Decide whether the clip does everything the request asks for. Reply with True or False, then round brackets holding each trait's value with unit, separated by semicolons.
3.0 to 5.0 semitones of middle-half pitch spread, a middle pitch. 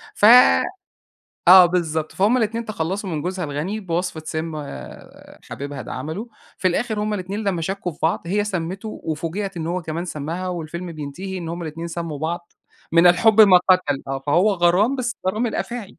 True (3.7 semitones; 180 Hz)